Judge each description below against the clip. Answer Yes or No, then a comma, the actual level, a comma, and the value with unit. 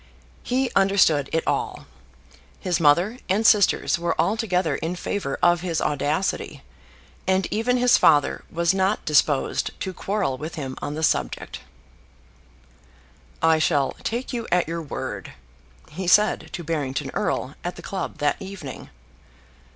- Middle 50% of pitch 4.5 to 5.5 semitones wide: Yes, average, 4.8 semitones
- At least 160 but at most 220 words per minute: No, average, 140 wpm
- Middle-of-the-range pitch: Yes, medium, 175 Hz